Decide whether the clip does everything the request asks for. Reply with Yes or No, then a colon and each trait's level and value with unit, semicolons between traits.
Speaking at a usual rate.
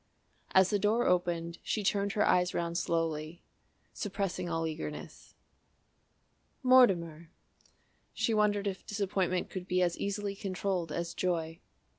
No: slow, 125 wpm